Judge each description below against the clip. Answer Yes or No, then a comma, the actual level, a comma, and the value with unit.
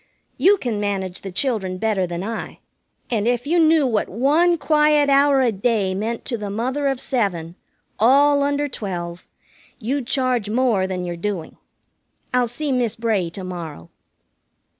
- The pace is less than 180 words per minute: Yes, average, 160 wpm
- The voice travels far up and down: Yes, wide, 6.3 semitones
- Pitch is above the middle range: Yes, high, 230 Hz